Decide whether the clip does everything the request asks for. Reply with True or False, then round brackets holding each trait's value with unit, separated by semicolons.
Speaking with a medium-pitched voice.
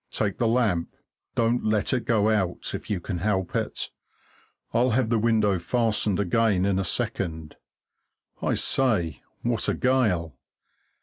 False (105 Hz)